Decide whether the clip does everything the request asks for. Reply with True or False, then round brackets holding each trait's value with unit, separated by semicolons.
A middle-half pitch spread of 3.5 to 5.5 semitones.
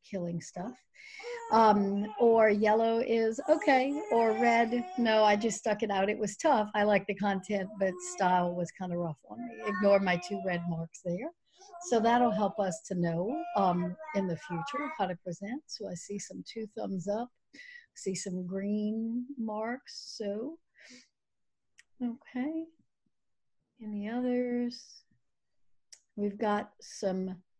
True (4.1 semitones)